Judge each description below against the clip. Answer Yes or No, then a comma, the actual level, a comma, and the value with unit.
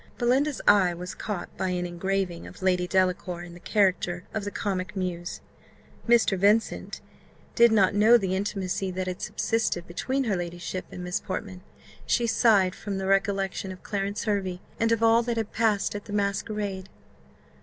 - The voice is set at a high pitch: Yes, high, 195 Hz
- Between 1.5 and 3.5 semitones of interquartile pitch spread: Yes, average, 2.7 semitones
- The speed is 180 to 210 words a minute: No, average, 170 wpm